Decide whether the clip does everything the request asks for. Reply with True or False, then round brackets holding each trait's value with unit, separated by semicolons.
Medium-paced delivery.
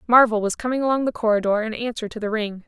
False (245 wpm)